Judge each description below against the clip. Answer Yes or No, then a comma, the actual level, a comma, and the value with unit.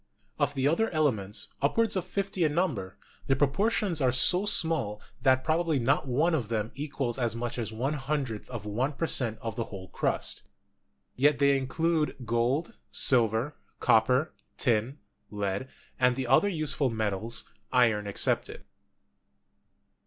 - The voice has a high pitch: No, low, 130 Hz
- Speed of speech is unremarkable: Yes, average, 145 wpm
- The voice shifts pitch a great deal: No, average, 5.0 semitones